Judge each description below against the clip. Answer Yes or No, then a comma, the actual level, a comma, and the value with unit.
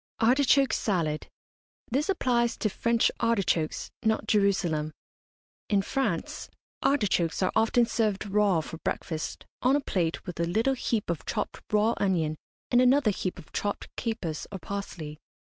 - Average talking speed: Yes, average, 145 wpm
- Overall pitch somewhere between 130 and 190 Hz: No, high, 205 Hz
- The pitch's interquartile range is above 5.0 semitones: Yes, wide, 5.5 semitones